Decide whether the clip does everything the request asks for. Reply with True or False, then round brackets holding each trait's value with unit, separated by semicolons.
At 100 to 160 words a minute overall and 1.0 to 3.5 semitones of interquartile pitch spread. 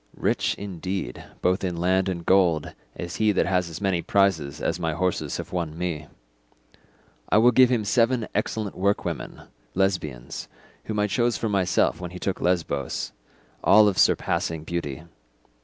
True (155 wpm; 3.2 semitones)